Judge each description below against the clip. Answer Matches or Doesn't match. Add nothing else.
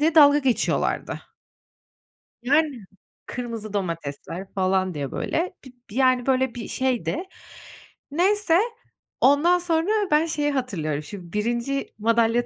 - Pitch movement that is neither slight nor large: Doesn't match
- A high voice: Matches